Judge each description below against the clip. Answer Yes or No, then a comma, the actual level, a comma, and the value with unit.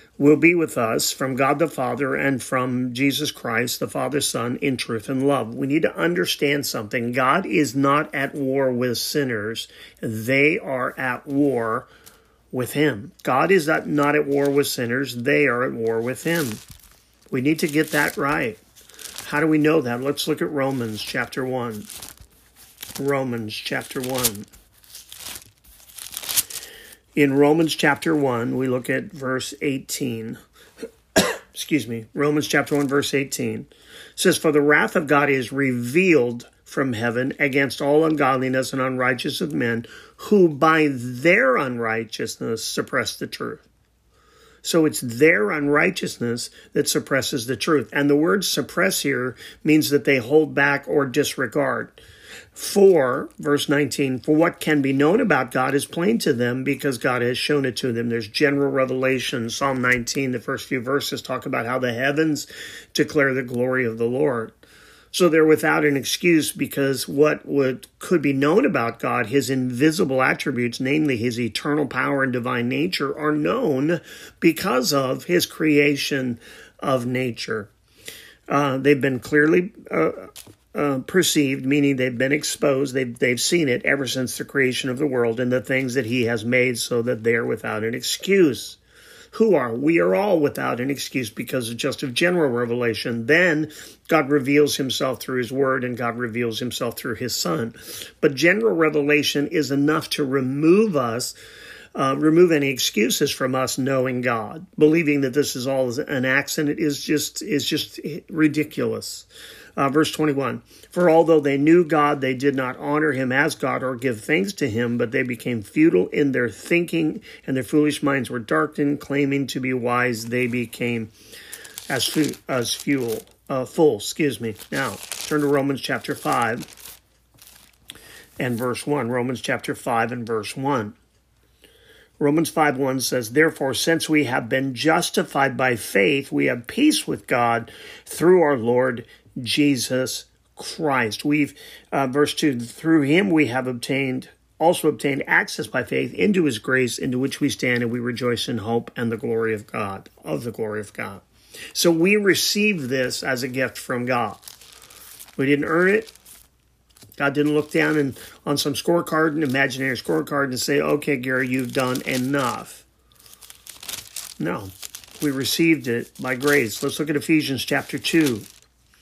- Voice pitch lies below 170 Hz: Yes, medium, 140 Hz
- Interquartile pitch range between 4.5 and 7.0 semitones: No, average, 3.1 semitones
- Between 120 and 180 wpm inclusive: Yes, average, 160 wpm